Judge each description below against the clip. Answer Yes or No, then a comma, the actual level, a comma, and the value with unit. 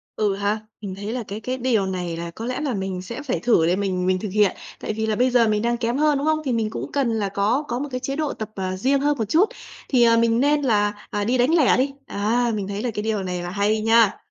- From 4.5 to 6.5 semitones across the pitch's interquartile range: No, average, 4.0 semitones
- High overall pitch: Yes, high, 220 Hz